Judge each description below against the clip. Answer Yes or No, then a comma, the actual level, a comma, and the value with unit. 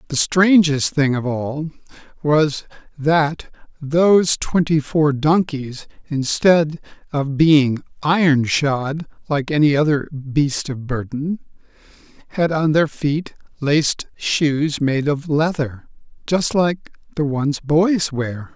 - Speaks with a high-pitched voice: No, medium, 150 Hz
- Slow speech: Yes, slow, 120 wpm